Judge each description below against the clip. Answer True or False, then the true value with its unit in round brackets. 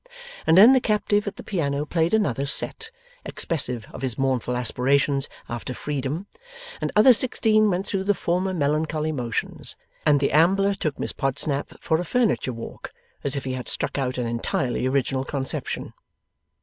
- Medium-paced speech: True (165 wpm)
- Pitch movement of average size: False (6.5 semitones)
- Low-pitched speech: False (145 Hz)